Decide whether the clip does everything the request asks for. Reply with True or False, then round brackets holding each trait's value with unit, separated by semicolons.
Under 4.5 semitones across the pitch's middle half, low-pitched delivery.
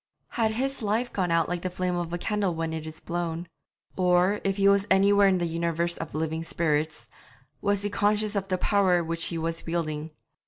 False (3.3 semitones; 175 Hz)